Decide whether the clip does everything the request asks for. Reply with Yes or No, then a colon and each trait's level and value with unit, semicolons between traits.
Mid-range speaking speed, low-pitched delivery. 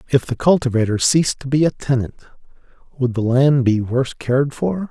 Yes: average, 185 wpm; low, 130 Hz